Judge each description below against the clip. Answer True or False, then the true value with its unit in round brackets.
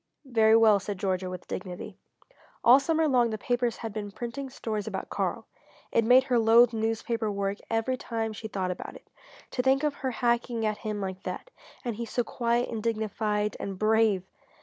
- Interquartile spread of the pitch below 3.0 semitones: True (2.6 semitones)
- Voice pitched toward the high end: True (225 Hz)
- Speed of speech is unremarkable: True (190 wpm)